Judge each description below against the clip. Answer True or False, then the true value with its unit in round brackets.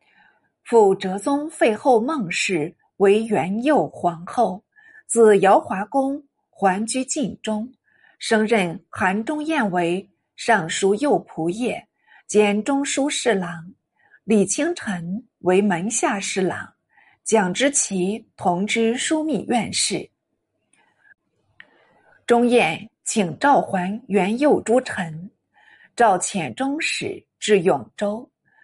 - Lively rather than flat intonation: True (6.0 semitones)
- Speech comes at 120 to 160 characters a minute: True (145 characters per minute)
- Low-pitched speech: False (220 Hz)